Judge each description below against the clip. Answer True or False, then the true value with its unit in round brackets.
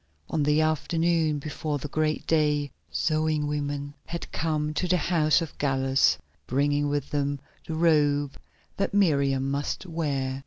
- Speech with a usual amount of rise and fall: False (1.7 semitones)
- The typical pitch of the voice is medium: True (150 Hz)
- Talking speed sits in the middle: True (145 wpm)